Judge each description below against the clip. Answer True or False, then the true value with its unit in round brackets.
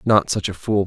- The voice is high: False (100 Hz)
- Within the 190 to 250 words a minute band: False (280 wpm)